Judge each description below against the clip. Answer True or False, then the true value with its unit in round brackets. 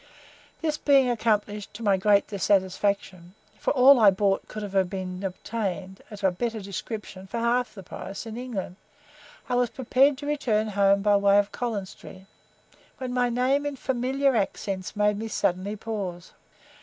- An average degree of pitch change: True (4.0 semitones)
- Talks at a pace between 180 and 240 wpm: False (165 wpm)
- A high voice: True (210 Hz)